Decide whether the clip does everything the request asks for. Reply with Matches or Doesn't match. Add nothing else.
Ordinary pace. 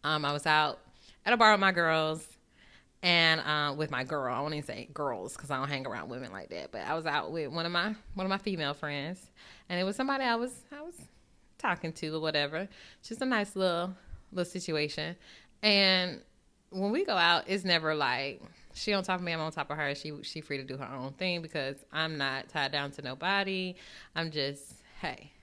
Doesn't match